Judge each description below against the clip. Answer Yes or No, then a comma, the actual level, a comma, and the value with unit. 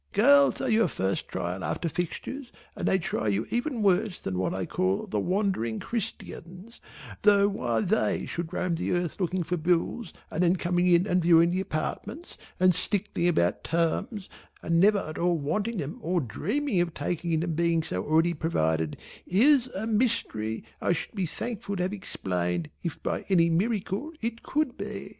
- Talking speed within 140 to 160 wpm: No, average, 175 wpm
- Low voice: No, medium, 175 Hz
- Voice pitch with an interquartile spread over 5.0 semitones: No, average, 4.6 semitones